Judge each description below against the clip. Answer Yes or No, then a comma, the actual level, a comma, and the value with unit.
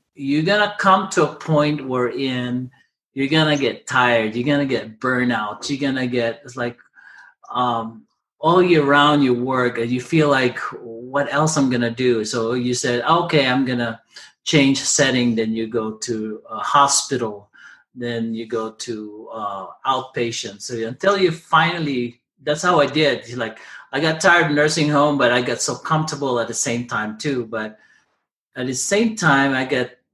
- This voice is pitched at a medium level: No, low, 130 Hz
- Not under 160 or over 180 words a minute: Yes, average, 175 wpm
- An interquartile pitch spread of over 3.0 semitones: Yes, average, 3.8 semitones